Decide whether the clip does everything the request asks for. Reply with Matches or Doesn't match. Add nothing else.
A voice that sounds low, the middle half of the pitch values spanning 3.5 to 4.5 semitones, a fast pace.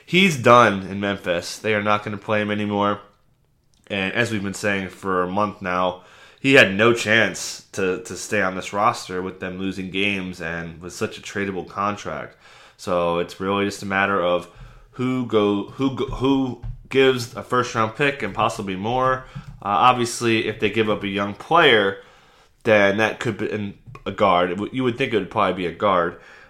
Doesn't match